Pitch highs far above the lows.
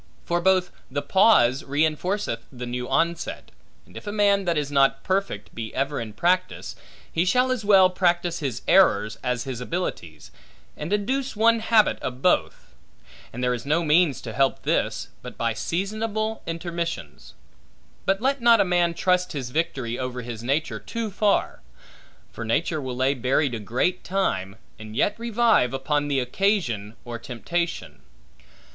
Yes: wide, 7.6 semitones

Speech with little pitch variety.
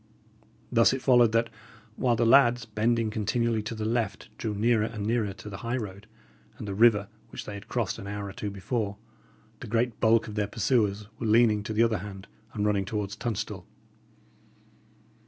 Yes: narrow, 2.2 semitones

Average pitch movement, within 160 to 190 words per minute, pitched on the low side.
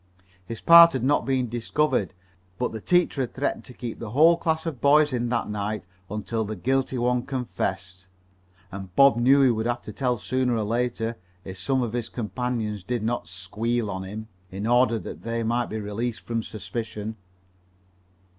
Yes: average, 3.2 semitones; average, 185 wpm; low, 115 Hz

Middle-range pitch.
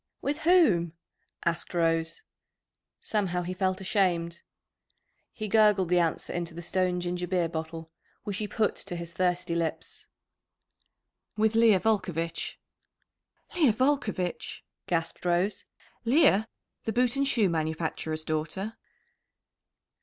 Yes: medium, 180 Hz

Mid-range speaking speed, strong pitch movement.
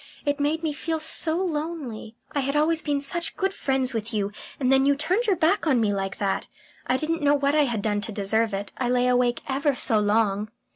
No: fast, 230 wpm; wide, 5.7 semitones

